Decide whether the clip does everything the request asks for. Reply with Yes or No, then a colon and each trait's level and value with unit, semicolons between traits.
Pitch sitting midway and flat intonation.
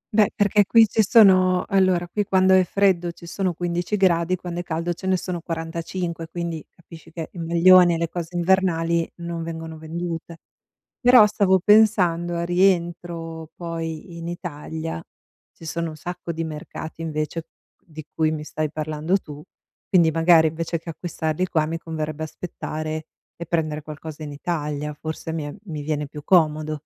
Yes: medium, 170 Hz; narrow, 2.1 semitones